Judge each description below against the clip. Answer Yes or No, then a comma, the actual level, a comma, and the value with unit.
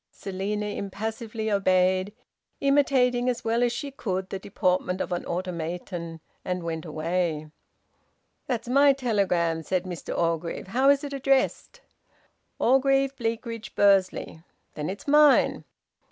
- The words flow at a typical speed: No, slow, 125 wpm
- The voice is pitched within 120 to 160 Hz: No, high, 200 Hz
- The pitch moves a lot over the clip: Yes, wide, 5.8 semitones